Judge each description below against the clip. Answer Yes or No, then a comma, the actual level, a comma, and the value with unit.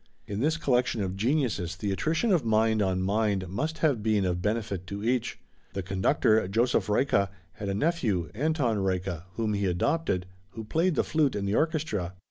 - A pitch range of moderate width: No, wide, 5.8 semitones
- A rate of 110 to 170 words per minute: No, average, 180 wpm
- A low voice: Yes, low, 105 Hz